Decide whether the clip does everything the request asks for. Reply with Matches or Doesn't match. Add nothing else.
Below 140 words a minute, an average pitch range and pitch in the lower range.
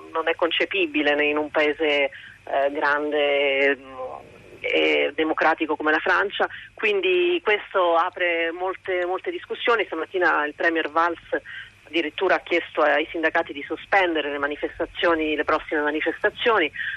Doesn't match